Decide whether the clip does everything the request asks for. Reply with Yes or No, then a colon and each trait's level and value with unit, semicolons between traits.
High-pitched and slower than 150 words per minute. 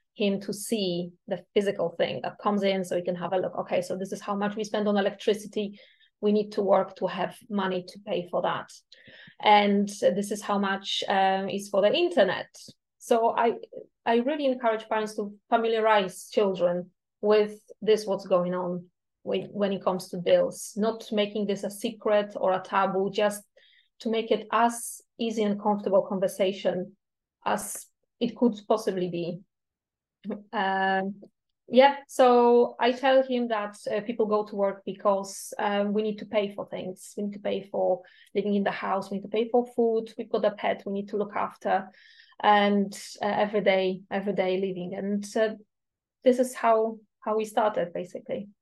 No: high, 205 Hz; average, 185 wpm